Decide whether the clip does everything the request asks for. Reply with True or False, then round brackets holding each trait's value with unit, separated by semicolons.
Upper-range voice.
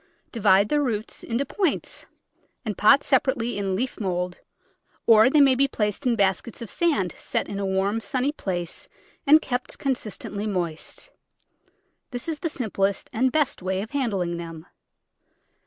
True (220 Hz)